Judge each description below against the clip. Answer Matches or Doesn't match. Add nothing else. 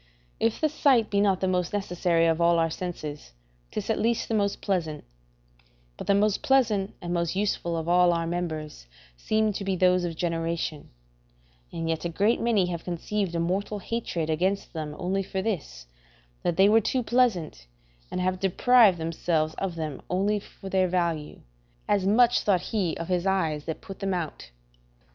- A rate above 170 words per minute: Matches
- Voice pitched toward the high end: Doesn't match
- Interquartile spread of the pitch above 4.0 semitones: Doesn't match